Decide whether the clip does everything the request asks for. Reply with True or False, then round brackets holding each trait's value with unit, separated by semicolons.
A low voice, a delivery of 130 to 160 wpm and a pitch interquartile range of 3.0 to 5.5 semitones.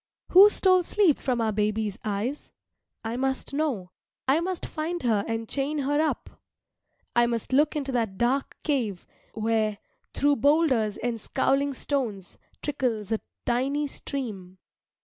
False (255 Hz; 140 wpm; 4.8 semitones)